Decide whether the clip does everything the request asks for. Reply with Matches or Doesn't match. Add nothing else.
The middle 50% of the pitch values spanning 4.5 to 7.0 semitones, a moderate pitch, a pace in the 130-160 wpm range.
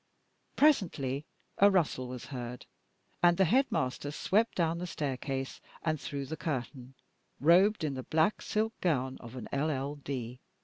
Matches